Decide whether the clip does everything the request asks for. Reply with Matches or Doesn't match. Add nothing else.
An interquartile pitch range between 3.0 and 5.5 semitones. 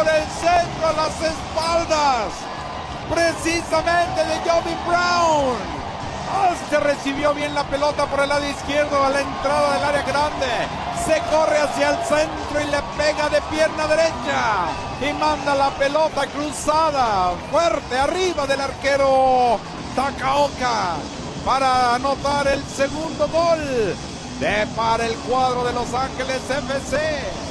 Doesn't match